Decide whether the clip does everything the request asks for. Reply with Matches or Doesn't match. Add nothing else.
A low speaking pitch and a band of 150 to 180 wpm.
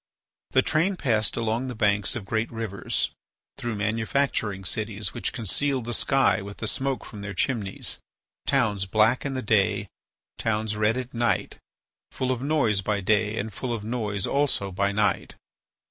Matches